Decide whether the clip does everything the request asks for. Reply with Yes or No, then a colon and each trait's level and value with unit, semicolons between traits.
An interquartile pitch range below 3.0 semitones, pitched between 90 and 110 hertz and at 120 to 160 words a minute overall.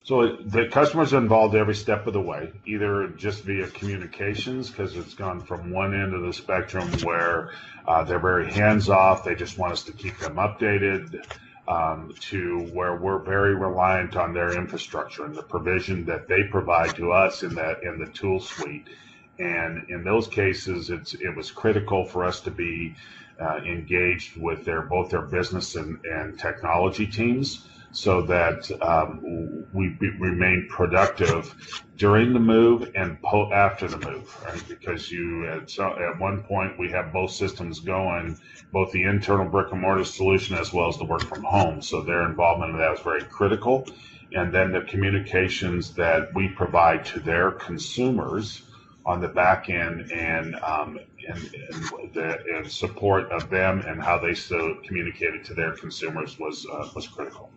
No: narrow, 2.5 semitones; very low, 95 Hz; average, 175 wpm